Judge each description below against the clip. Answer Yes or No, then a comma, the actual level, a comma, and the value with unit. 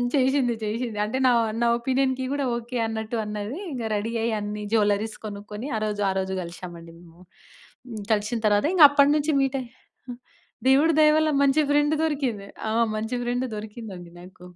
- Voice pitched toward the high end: Yes, high, 225 Hz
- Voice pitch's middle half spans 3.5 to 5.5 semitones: Yes, average, 4.4 semitones